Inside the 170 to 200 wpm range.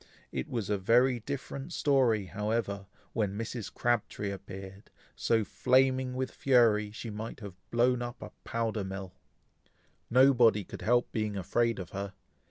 No: average, 145 wpm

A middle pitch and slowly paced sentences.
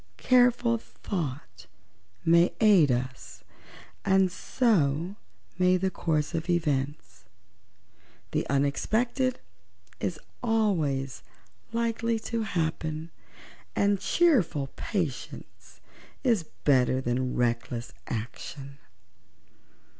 Yes: medium, 165 Hz; slow, 80 wpm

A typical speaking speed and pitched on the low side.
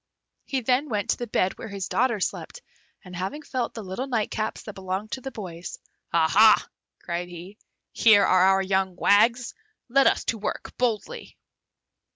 No: average, 170 wpm; high, 210 Hz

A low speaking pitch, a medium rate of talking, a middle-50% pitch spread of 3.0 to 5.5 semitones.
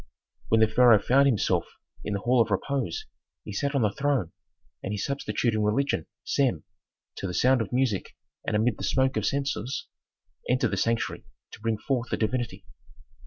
Yes: low, 120 Hz; average, 180 wpm; average, 4.0 semitones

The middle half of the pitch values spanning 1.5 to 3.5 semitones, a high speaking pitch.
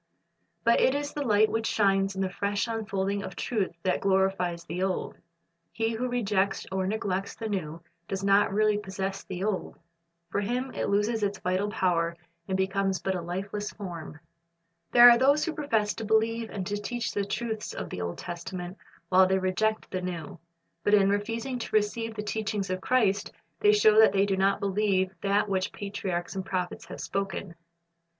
Yes: narrow, 2.4 semitones; high, 200 Hz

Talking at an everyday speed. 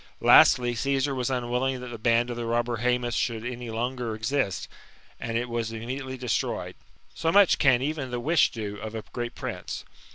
Yes: average, 185 wpm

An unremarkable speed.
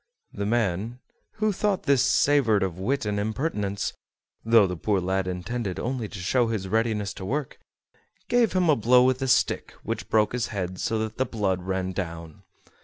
Yes: average, 180 wpm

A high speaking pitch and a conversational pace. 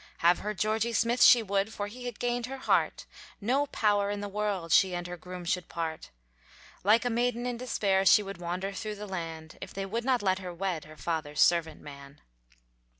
No: high, 195 Hz; fast, 210 wpm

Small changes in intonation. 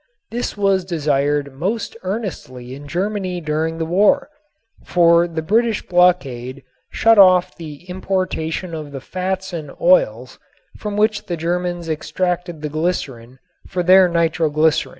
No: average, 3.4 semitones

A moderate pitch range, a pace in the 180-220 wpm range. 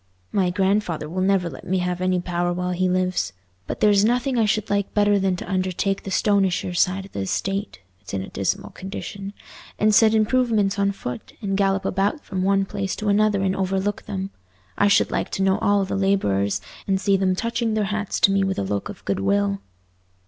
No: narrow, 2.0 semitones; average, 200 wpm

